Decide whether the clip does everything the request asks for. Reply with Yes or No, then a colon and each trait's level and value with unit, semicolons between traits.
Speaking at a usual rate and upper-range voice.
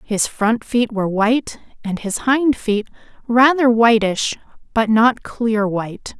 Yes: average, 145 wpm; high, 225 Hz